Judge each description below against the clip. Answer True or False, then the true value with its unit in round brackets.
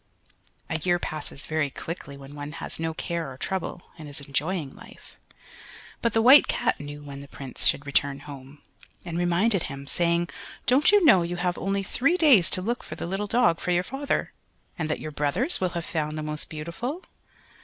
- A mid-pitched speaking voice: True (170 Hz)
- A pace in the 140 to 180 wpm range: False (195 wpm)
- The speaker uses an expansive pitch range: False (4.7 semitones)